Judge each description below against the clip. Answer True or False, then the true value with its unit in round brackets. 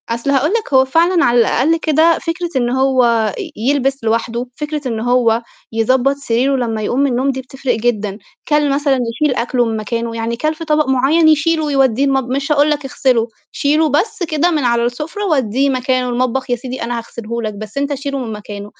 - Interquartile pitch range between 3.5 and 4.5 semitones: True (3.9 semitones)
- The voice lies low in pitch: False (260 Hz)